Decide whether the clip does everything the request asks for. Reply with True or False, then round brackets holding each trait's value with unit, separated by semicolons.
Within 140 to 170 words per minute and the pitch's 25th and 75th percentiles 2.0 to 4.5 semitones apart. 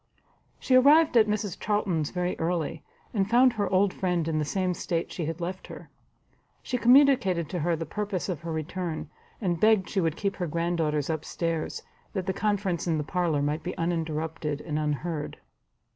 False (185 wpm; 3.8 semitones)